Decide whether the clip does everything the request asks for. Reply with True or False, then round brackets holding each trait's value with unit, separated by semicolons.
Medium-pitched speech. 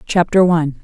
True (170 Hz)